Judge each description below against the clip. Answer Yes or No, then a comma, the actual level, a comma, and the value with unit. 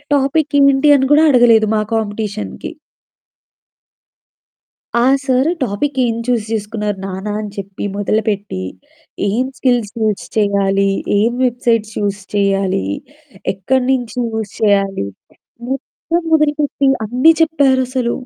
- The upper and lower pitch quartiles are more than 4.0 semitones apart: Yes, average, 4.4 semitones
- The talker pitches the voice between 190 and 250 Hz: Yes, high, 225 Hz